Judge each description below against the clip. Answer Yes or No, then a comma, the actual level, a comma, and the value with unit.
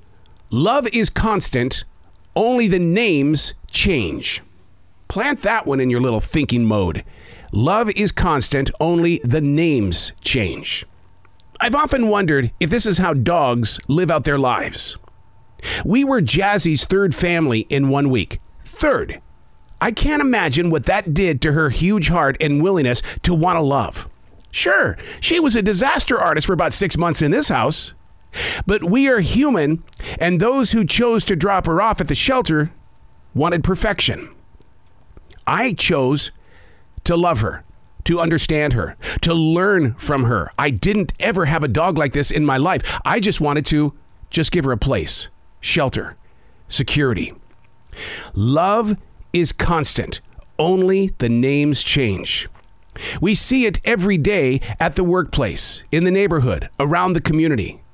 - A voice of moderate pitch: Yes, medium, 150 Hz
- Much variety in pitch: Yes, wide, 7.7 semitones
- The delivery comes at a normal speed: Yes, average, 150 wpm